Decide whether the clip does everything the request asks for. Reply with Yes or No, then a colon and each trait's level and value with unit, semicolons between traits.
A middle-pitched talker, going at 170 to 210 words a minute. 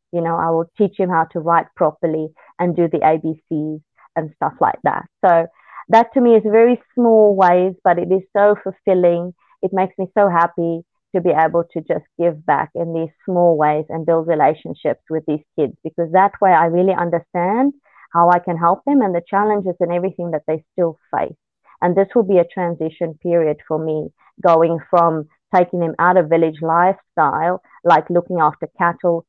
Yes: medium, 170 Hz; average, 195 wpm